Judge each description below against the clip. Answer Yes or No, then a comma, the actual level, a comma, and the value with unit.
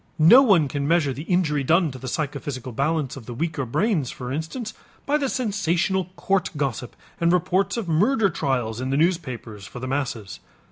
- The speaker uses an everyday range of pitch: No, wide, 6.0 semitones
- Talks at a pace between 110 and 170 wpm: No, average, 185 wpm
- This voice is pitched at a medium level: Yes, medium, 155 Hz